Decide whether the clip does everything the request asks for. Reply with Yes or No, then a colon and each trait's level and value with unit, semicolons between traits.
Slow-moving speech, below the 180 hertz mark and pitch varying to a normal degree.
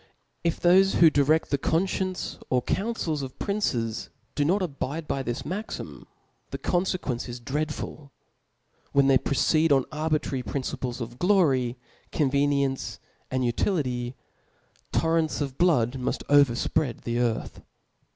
Yes: slow, 125 wpm; medium, 140 Hz; average, 4.3 semitones